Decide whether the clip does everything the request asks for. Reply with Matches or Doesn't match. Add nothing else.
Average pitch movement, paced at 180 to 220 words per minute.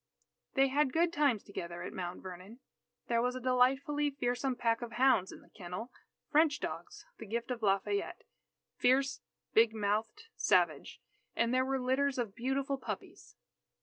Doesn't match